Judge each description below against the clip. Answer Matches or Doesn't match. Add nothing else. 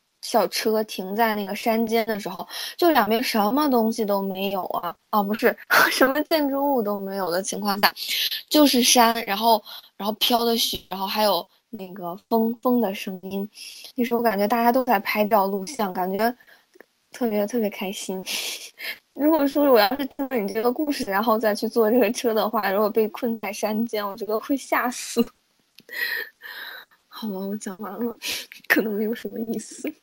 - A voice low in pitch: Doesn't match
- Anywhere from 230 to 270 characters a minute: Matches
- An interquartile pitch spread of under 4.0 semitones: Matches